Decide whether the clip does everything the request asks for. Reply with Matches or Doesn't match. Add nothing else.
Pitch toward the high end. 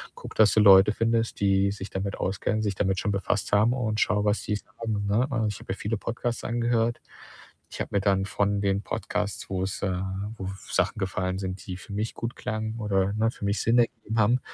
Doesn't match